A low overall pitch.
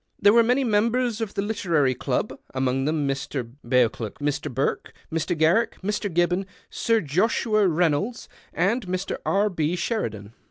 No: medium, 175 Hz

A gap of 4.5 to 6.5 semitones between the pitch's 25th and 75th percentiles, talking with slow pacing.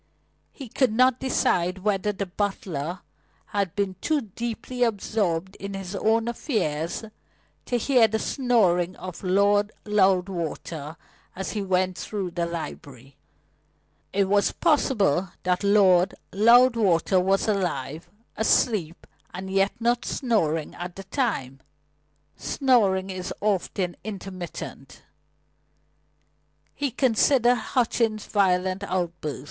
No: average, 3.7 semitones; slow, 110 wpm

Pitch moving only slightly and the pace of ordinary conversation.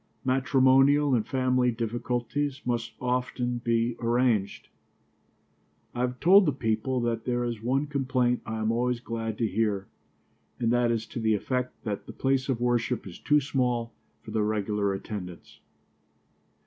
Yes: narrow, 2.3 semitones; average, 150 wpm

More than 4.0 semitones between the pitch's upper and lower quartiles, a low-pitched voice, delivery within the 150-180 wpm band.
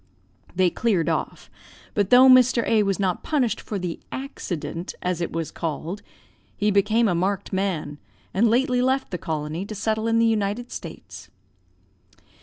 No: average, 4.4 semitones; high, 200 Hz; average, 160 wpm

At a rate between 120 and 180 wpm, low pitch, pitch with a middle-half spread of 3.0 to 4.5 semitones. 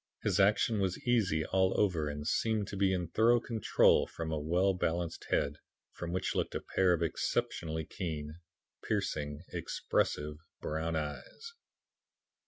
Yes: average, 145 wpm; very low, 85 Hz; average, 4.0 semitones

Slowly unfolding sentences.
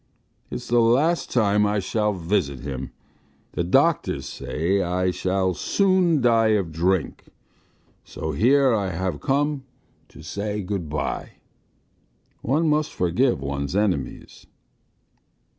Yes: slow, 120 wpm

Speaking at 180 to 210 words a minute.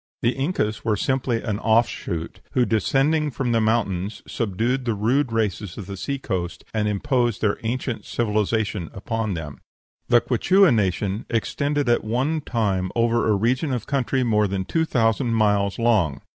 No: average, 160 wpm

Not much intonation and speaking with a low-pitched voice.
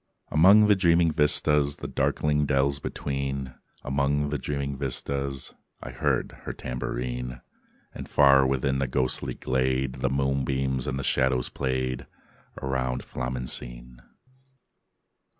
Yes: narrow, 1.6 semitones; very low, 65 Hz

